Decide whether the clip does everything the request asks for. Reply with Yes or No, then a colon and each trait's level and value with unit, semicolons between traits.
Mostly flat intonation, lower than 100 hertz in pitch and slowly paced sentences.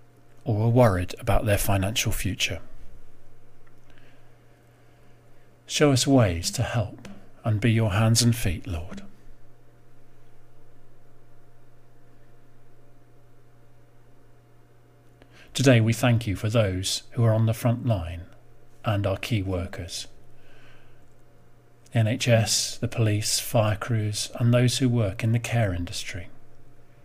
No: narrow, 1.1 semitones; low, 115 Hz; slow, 110 wpm